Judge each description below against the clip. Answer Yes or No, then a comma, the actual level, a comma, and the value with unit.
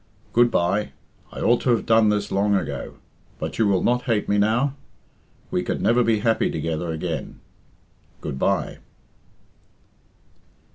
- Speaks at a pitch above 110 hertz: No, low, 105 Hz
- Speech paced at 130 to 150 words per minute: Yes, average, 145 wpm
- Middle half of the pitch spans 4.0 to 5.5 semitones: No, average, 3.6 semitones